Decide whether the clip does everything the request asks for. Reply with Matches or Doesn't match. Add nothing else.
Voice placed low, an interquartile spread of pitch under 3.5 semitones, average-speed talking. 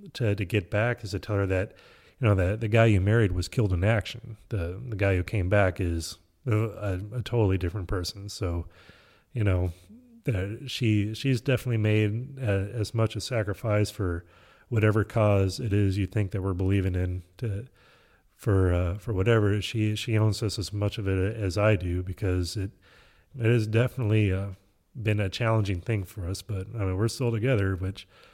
Matches